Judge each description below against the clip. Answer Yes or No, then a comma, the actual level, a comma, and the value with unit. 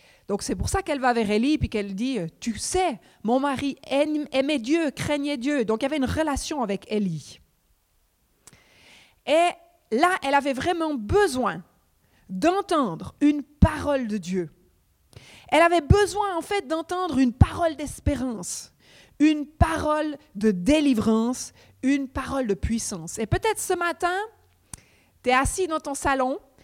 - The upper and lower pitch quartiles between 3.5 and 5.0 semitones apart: No, wide, 5.6 semitones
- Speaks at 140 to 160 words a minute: Yes, slow, 145 wpm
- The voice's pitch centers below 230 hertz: No, very high, 280 Hz